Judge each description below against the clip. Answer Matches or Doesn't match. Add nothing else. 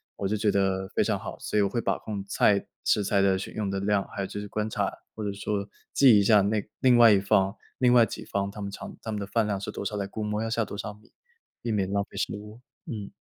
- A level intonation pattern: Matches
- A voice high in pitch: Doesn't match